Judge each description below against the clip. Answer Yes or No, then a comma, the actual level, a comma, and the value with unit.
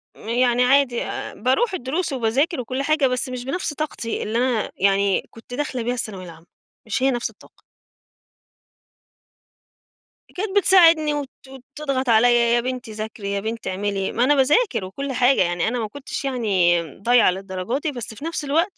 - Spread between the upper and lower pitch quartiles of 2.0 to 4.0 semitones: No, average, 4.4 semitones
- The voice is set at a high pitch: Yes, high, 245 Hz